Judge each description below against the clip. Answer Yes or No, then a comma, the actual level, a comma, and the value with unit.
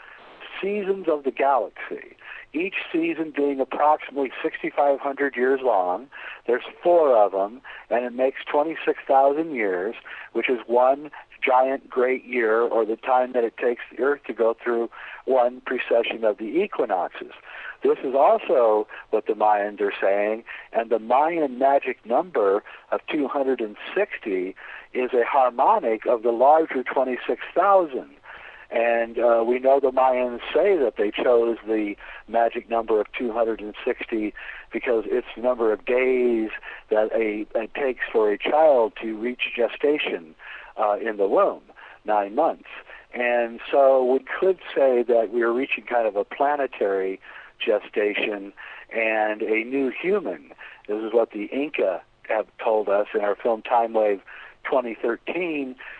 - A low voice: Yes, low, 125 Hz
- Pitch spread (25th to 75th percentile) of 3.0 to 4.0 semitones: No, average, 4.7 semitones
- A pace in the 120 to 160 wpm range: Yes, average, 145 wpm